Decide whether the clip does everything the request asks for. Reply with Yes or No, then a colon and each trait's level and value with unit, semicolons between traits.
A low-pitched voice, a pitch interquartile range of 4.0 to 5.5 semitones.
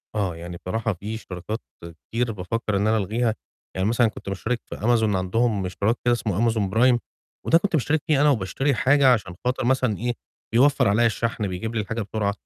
No: low, 110 Hz; average, 3.4 semitones